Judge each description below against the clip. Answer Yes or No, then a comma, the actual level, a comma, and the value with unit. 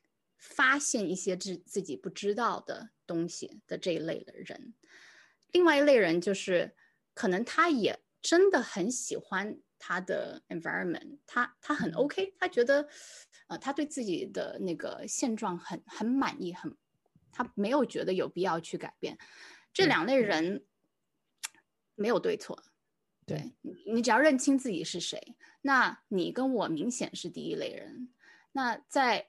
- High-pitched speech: Yes, very high, 260 Hz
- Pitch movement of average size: No, wide, 6.6 semitones